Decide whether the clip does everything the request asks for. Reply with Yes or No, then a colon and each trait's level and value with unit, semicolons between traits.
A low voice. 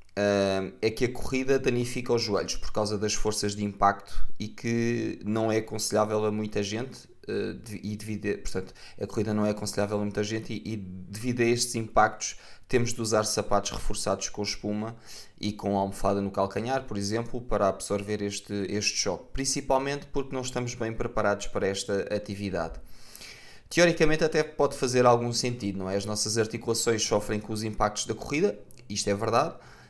Yes: low, 105 Hz